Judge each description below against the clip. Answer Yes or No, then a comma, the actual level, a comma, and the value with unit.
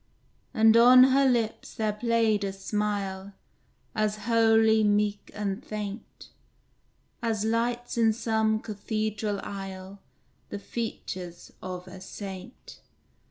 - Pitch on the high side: Yes, high, 215 Hz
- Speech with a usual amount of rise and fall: No, narrow, 2.2 semitones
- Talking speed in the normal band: No, slow, 110 wpm